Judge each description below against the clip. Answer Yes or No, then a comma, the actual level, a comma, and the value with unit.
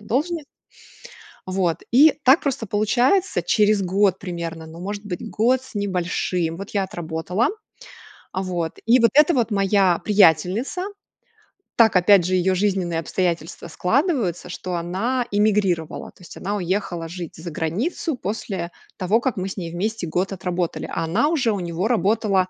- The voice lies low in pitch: No, high, 190 Hz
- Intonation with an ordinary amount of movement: Yes, average, 4.2 semitones